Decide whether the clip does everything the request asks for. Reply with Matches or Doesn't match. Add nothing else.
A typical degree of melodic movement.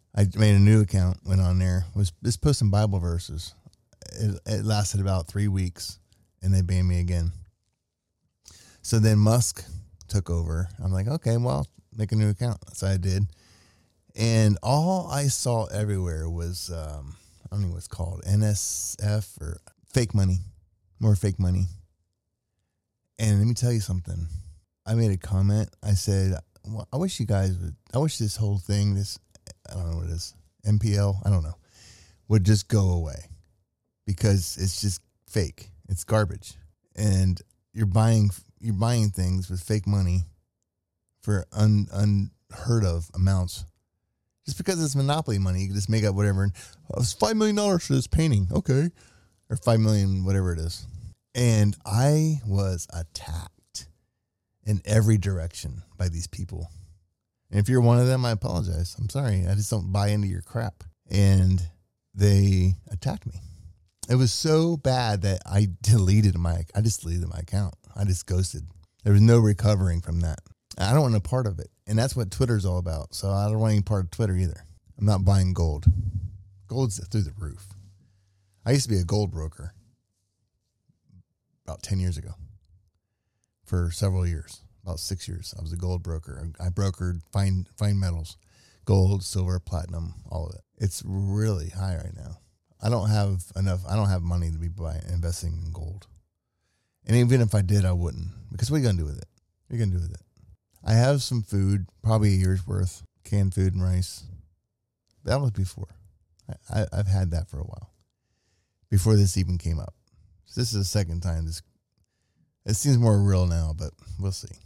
Matches